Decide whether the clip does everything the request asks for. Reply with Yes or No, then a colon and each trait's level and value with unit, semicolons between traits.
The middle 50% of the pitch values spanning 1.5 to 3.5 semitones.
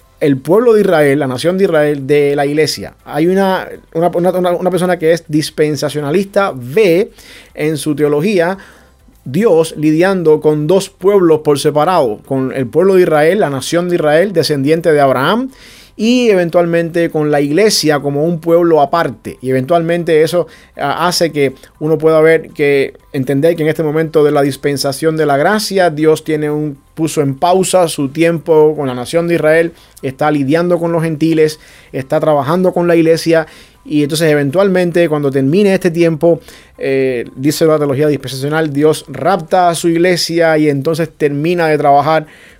Yes: average, 2.7 semitones